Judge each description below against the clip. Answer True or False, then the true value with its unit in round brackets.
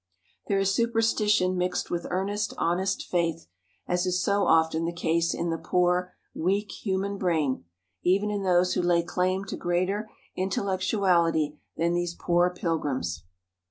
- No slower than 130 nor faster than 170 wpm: True (145 wpm)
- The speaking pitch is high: False (180 Hz)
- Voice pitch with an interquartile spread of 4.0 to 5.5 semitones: False (2.4 semitones)